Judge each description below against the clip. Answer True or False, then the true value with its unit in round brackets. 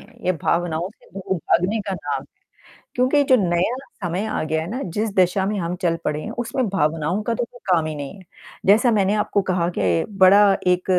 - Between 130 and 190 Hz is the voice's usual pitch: True (185 Hz)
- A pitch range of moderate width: True (4.1 semitones)